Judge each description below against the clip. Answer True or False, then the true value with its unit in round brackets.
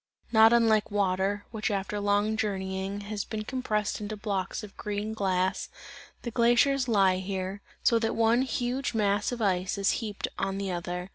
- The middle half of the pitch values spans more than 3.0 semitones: False (2.4 semitones)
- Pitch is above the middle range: True (205 Hz)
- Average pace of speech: True (165 wpm)